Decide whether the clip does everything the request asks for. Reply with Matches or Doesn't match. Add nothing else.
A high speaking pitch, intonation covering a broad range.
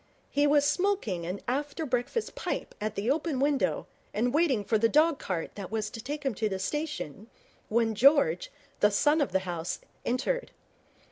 Matches